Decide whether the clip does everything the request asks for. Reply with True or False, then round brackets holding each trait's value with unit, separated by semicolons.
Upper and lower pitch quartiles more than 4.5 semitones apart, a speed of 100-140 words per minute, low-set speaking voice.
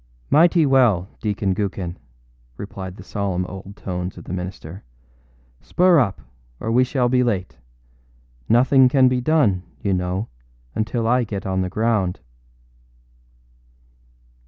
True (5.1 semitones; 135 wpm; 105 Hz)